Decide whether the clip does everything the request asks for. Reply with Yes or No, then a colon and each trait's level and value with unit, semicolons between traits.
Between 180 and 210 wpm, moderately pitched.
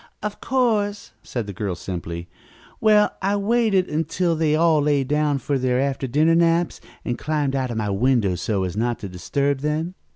Yes: average, 185 wpm; medium, 145 Hz